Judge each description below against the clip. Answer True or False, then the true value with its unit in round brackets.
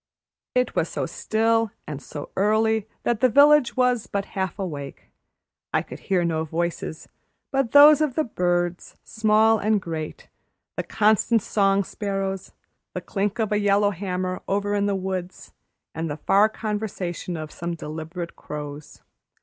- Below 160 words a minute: True (150 wpm)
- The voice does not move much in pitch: False (4.0 semitones)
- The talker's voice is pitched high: True (200 Hz)